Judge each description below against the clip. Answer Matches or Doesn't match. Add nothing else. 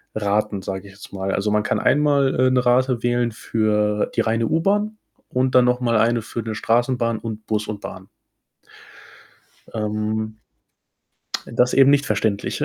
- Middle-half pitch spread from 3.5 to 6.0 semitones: Doesn't match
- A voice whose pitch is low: Matches